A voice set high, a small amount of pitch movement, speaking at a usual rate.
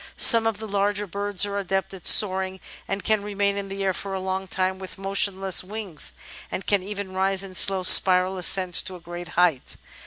No: high, 195 Hz; narrow, 1.3 semitones; fast, 210 wpm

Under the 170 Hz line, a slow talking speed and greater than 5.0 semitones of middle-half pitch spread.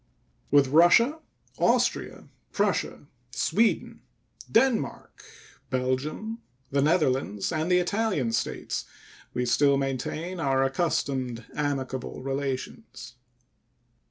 Yes: medium, 140 Hz; slow, 85 wpm; wide, 5.4 semitones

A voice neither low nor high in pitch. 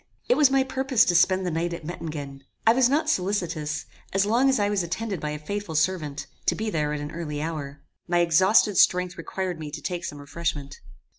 Yes: medium, 175 Hz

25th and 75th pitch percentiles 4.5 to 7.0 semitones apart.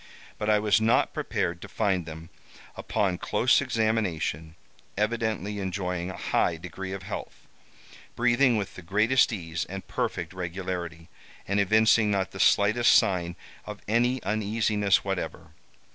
No: average, 3.5 semitones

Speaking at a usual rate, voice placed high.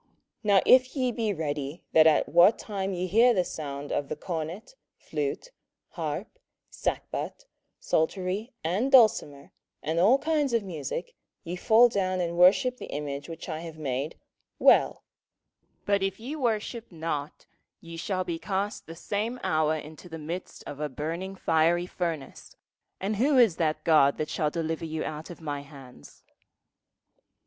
No: average, 160 wpm; medium, 175 Hz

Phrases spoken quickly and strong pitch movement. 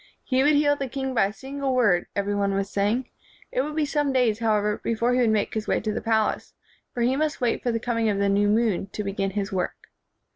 No: fast, 250 wpm; average, 4.4 semitones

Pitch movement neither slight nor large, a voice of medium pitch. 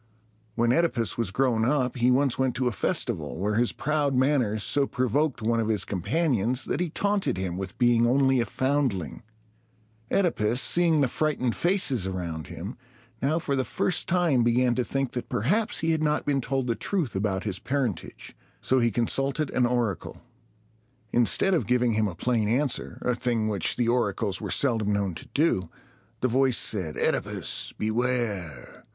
No: average, 4.5 semitones; low, 125 Hz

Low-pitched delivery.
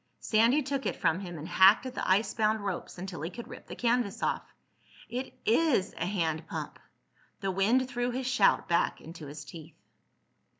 No: high, 200 Hz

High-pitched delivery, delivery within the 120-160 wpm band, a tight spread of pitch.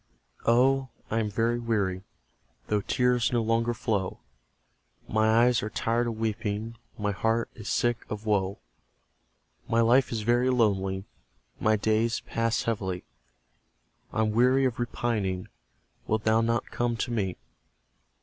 No: low, 115 Hz; slow, 135 wpm; narrow, 2.0 semitones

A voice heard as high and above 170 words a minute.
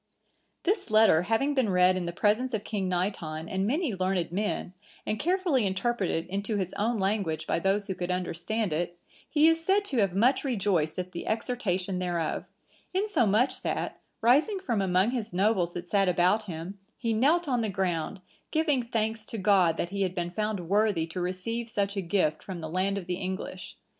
Yes: high, 200 Hz; average, 190 wpm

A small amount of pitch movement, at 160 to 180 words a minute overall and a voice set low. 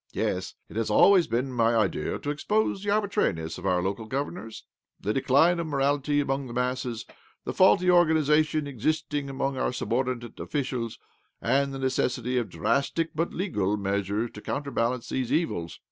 No: average, 4.8 semitones; average, 170 wpm; low, 130 Hz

